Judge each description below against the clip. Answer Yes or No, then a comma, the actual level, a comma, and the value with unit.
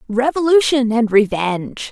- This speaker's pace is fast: No, slow, 95 wpm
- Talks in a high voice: Yes, high, 240 Hz